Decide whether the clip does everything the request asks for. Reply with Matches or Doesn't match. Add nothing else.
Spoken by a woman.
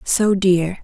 Matches